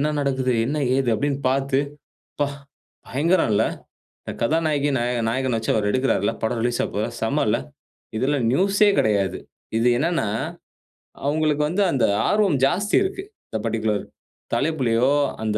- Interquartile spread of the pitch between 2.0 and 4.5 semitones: No, average, 4.9 semitones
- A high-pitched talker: No, low, 135 Hz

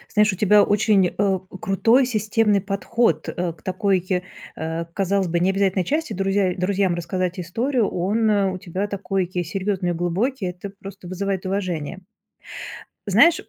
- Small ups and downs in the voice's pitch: Yes, narrow, 2.3 semitones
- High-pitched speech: Yes, high, 195 Hz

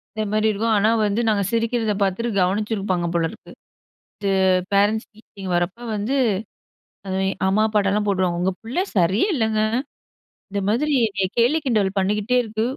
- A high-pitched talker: Yes, high, 210 Hz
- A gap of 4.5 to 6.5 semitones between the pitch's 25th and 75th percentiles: No, narrow, 2.4 semitones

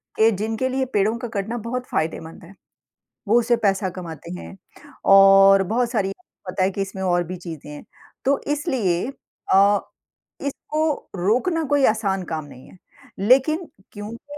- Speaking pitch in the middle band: No, high, 205 Hz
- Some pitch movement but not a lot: Yes, average, 5.0 semitones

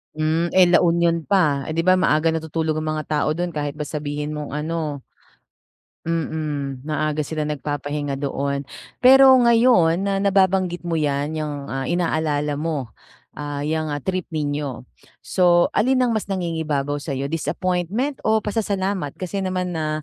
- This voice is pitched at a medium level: Yes, medium, 160 Hz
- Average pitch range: Yes, average, 3.7 semitones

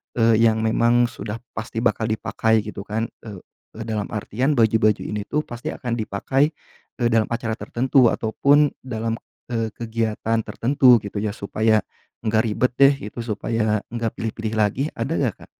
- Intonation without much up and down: Yes, narrow, 1.7 semitones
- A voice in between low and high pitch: No, low, 115 Hz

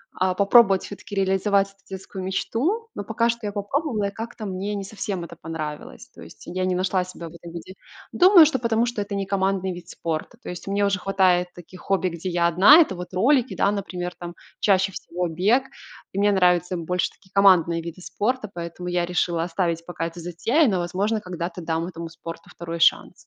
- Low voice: No, medium, 185 Hz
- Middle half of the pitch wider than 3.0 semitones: No, average, 2.7 semitones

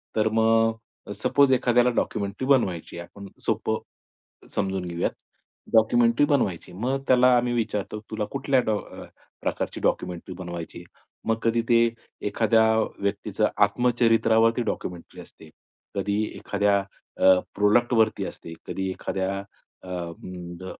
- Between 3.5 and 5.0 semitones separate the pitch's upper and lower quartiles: Yes, average, 3.8 semitones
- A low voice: Yes, low, 110 Hz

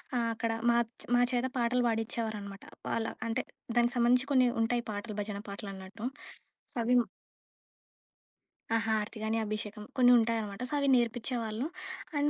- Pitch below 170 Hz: No, high, 230 Hz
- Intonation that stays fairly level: Yes, narrow, 2.1 semitones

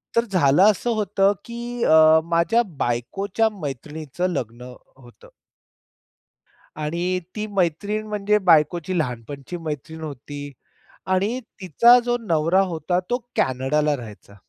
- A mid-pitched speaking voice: Yes, medium, 170 Hz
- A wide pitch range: Yes, wide, 5.8 semitones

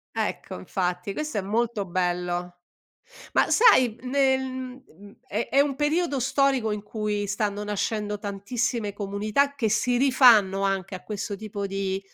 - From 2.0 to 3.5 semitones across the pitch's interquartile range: No, average, 4.5 semitones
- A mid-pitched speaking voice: No, high, 210 Hz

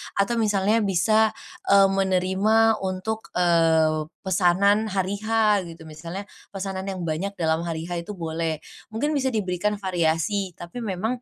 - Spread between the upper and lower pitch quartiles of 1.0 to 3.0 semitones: No, average, 3.6 semitones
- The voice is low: No, high, 190 Hz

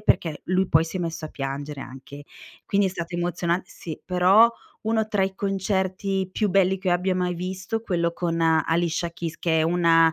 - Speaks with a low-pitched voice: No, medium, 180 Hz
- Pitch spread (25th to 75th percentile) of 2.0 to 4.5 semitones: Yes, narrow, 2.5 semitones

